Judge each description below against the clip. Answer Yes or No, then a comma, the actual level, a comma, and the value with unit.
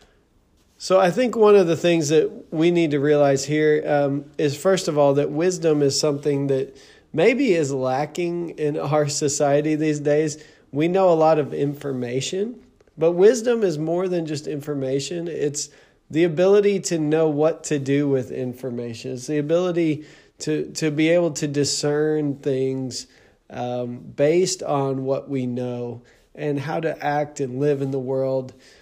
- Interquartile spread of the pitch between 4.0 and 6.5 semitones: No, average, 3.2 semitones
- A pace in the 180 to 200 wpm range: No, average, 165 wpm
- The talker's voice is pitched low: No, medium, 150 Hz